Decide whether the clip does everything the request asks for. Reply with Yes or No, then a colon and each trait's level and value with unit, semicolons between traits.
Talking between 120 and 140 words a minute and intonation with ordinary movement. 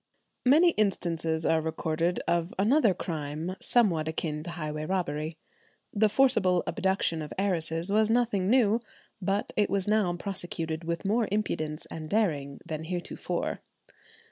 Yes: slow, 135 wpm; average, 4.6 semitones